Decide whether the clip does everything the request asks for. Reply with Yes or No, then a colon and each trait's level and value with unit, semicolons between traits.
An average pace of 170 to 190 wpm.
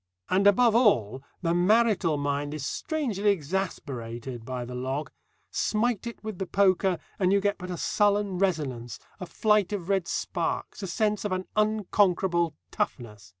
No: average, 155 wpm